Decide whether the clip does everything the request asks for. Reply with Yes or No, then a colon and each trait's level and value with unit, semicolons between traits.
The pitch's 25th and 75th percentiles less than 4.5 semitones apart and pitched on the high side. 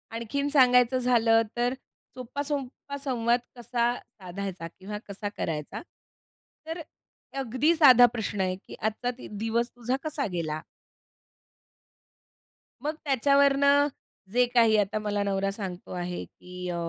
No: average, 5.0 semitones; high, 235 Hz